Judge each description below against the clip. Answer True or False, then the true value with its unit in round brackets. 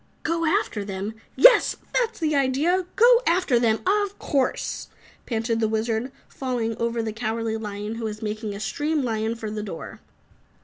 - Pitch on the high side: True (230 Hz)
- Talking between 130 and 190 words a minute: True (165 wpm)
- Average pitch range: False (6.2 semitones)